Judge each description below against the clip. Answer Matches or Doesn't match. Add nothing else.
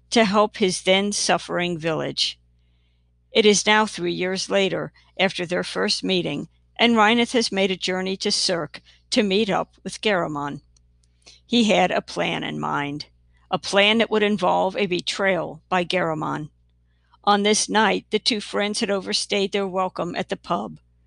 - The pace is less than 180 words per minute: Matches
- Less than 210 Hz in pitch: Matches